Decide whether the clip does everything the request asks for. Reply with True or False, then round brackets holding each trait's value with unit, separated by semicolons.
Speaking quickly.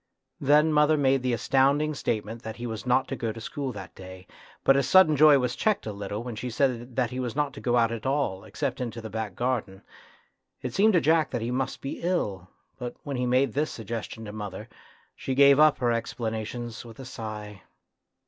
True (215 wpm)